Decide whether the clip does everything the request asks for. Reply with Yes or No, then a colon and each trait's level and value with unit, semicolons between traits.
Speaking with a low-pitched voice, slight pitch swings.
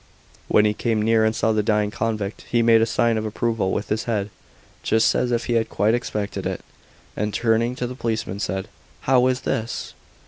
Yes: low, 110 Hz; narrow, 1.7 semitones